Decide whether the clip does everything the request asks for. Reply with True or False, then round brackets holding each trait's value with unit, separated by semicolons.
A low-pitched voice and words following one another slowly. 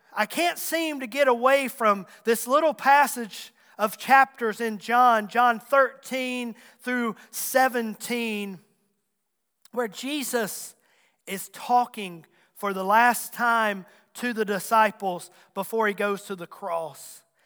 False (225 Hz; 120 wpm)